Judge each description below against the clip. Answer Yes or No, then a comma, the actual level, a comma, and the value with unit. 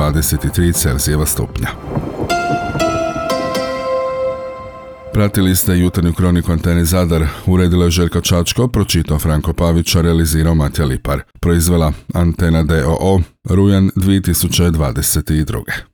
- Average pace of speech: No, slow, 90 wpm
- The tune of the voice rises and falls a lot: No, average, 3.4 semitones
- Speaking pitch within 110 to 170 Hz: No, very low, 85 Hz